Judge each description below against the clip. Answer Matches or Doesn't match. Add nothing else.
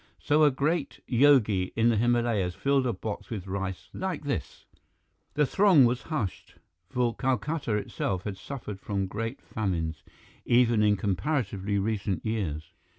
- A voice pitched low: Matches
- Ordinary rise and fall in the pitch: Doesn't match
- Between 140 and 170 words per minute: Matches